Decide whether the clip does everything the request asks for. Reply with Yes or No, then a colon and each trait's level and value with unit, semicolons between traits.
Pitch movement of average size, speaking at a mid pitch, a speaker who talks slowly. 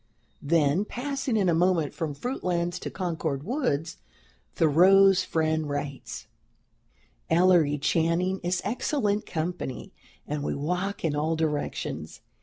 Yes: average, 3.8 semitones; medium, 170 Hz; slow, 115 wpm